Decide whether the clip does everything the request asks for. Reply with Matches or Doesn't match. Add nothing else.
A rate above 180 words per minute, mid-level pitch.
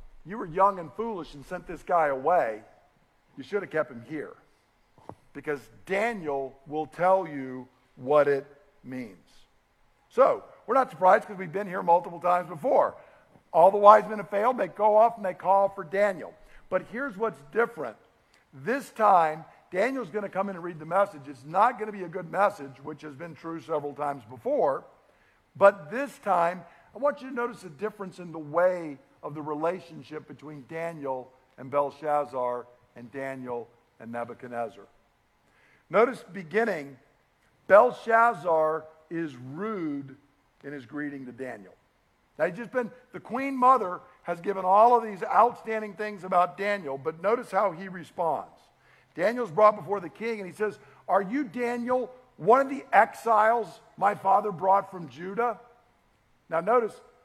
Doesn't match